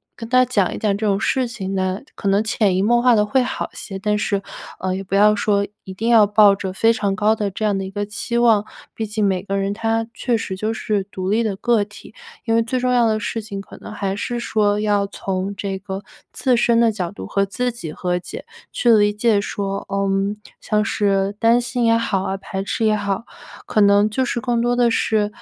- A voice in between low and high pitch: No, high, 210 Hz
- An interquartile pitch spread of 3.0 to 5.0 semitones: No, narrow, 2.5 semitones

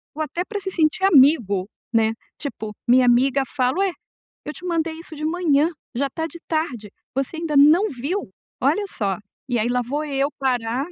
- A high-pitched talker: Yes, very high, 285 Hz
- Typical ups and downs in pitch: Yes, average, 4.9 semitones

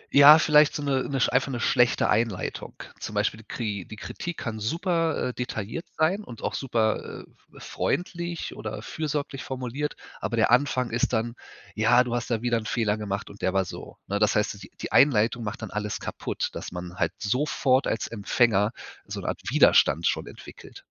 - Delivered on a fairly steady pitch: No, average, 4.8 semitones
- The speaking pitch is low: Yes, low, 120 Hz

